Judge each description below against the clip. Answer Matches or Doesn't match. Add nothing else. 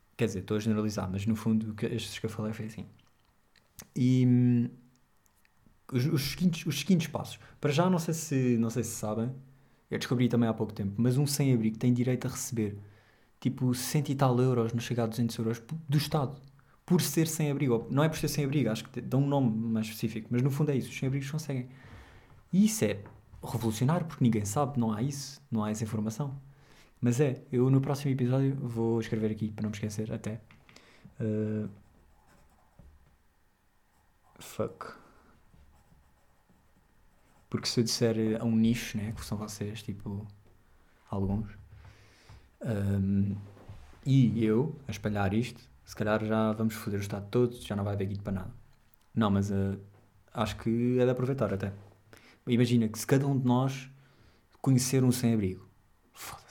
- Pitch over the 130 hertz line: Doesn't match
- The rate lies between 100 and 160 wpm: Doesn't match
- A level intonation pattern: Doesn't match